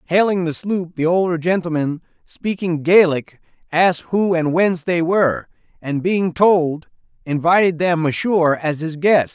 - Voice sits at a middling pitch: Yes, medium, 170 Hz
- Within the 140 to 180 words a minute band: Yes, average, 150 wpm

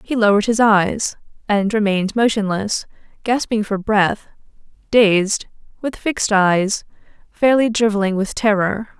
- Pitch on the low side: No, high, 210 Hz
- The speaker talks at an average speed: No, slow, 115 wpm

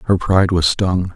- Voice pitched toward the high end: No, very low, 90 Hz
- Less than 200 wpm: No, fast, 210 wpm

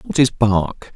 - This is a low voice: Yes, low, 120 Hz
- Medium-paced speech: Yes, average, 190 wpm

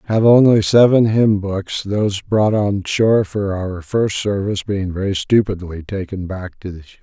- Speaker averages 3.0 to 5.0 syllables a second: Yes, 4.6 syllables/s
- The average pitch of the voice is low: Yes, low, 100 Hz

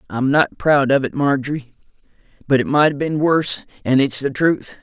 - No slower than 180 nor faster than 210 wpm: Yes, average, 200 wpm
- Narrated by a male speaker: Yes, male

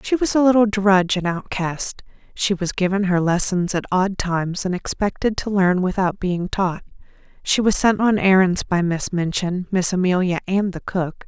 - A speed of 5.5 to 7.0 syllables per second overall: No, 4.7 syllables/s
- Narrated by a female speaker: Yes, female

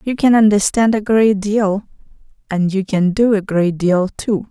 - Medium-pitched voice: No, high, 205 Hz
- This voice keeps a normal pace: Yes, average, 185 wpm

